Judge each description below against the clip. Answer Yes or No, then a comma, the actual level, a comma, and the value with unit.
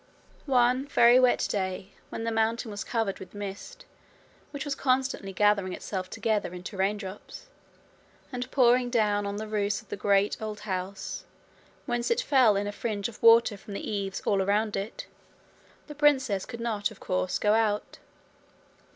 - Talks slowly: No, average, 170 wpm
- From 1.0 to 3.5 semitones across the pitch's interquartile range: Yes, average, 3.2 semitones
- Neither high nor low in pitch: No, high, 215 Hz